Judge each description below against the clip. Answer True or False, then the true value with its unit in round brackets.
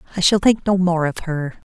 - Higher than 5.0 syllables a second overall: True (5.4 syllables/s)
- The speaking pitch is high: False (175 Hz)